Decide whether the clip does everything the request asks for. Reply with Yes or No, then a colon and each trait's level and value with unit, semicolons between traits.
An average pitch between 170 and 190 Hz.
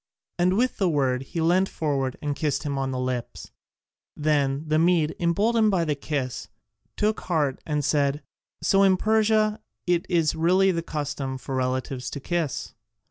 No: medium, 155 Hz